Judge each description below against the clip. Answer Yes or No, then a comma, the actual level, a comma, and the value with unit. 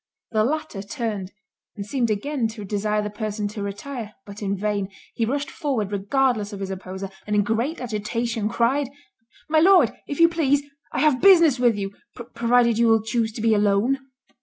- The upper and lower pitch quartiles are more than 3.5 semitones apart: Yes, average, 4.4 semitones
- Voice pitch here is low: No, high, 225 Hz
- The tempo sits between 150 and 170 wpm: No, average, 185 wpm